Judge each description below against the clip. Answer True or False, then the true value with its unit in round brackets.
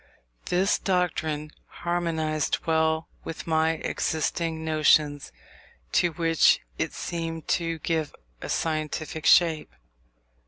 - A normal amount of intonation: False (1.2 semitones)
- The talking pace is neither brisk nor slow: False (95 wpm)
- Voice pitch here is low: False (160 Hz)